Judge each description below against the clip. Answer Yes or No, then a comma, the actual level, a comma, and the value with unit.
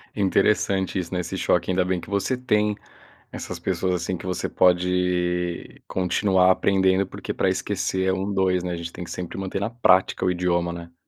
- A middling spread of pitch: No, narrow, 1.5 semitones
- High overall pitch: No, very low, 90 Hz